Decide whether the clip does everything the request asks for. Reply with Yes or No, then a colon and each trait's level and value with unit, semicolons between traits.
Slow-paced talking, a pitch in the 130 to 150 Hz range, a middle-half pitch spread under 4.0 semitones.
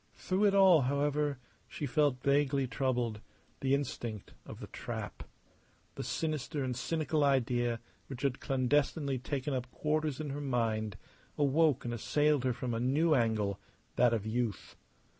No: average, 150 wpm; low, 135 Hz; average, 3.4 semitones